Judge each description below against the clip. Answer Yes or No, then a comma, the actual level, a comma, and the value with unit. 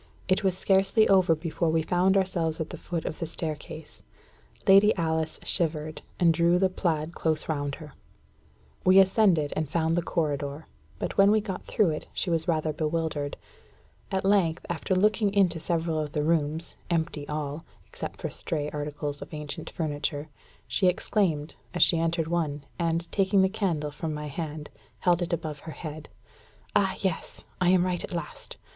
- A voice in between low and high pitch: Yes, medium, 165 Hz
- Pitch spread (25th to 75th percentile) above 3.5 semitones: No, average, 3.2 semitones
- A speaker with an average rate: Yes, average, 175 wpm